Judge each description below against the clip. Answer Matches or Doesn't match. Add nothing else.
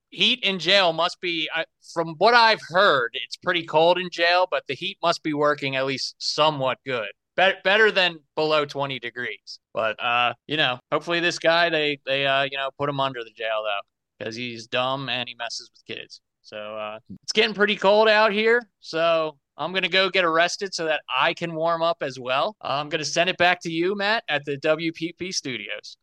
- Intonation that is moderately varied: Matches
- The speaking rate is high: Matches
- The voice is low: Doesn't match